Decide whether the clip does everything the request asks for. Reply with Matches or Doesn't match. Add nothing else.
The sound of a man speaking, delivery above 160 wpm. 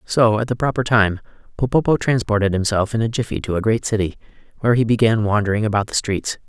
Matches